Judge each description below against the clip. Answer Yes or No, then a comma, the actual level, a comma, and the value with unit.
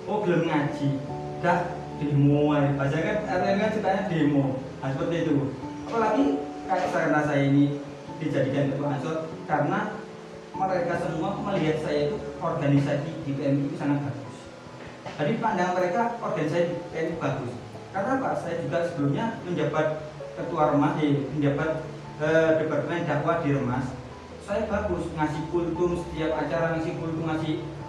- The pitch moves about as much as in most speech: Yes, average, 3.0 semitones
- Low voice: No, medium, 155 Hz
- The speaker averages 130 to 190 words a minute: Yes, fast, 140 wpm